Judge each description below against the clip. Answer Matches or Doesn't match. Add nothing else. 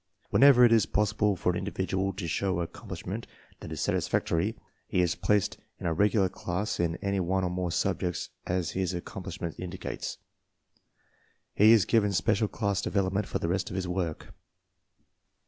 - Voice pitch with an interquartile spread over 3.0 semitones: Doesn't match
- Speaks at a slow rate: Doesn't match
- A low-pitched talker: Matches